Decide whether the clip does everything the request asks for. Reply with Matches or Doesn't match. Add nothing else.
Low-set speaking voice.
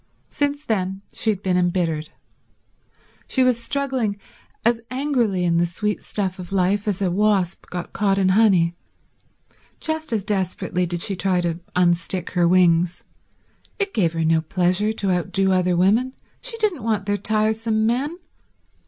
Doesn't match